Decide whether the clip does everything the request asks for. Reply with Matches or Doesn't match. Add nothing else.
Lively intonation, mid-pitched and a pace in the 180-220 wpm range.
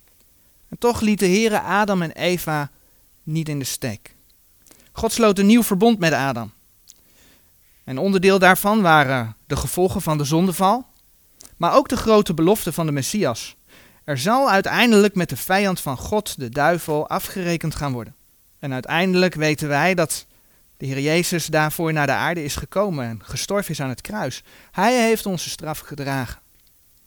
Doesn't match